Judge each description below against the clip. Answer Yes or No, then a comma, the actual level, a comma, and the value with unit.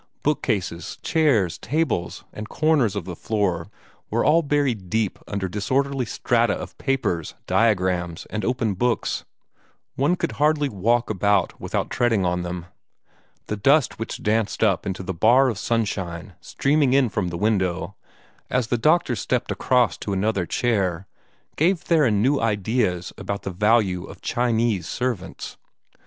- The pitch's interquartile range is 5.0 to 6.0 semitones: Yes, average, 5.3 semitones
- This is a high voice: No, low, 110 Hz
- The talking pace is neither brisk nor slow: Yes, average, 145 wpm